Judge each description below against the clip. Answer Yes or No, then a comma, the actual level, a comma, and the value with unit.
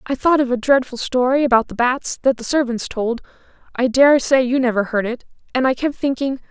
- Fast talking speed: Yes, fast, 210 wpm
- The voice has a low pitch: No, very high, 255 Hz